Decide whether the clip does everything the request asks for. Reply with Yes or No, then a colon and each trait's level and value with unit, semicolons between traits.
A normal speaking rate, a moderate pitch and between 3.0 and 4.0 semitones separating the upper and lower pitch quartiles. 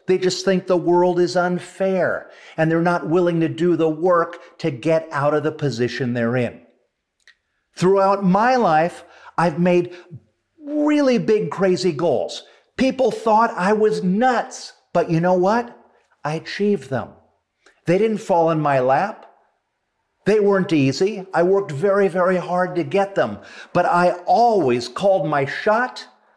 Yes: average, 150 wpm; medium, 180 Hz; average, 3.7 semitones